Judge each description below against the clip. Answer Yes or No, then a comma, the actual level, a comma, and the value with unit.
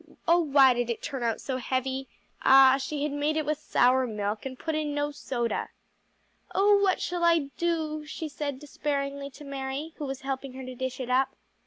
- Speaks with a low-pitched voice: No, very high, 275 Hz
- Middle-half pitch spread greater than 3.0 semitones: No, average, 2.7 semitones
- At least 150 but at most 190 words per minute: No, average, 200 wpm